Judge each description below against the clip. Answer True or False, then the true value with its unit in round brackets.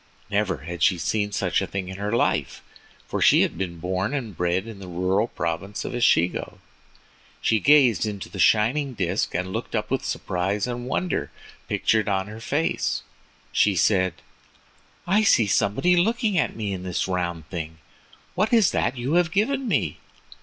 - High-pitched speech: False (105 Hz)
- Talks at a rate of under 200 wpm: True (175 wpm)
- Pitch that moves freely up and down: True (5.8 semitones)